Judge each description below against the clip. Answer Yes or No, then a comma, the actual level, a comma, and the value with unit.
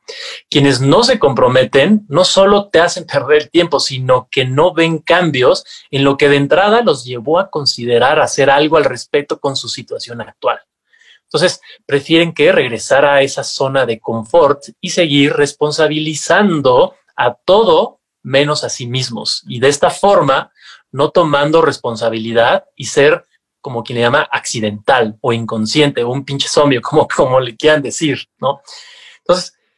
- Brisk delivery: No, average, 155 wpm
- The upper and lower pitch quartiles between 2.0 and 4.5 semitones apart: No, average, 5.3 semitones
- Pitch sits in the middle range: Yes, medium, 145 Hz